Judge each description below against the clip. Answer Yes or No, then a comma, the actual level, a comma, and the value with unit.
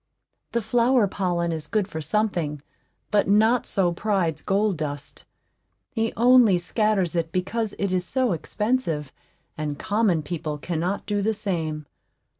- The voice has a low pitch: No, high, 190 Hz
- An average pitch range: Yes, average, 4.9 semitones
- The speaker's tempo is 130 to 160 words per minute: Yes, average, 140 wpm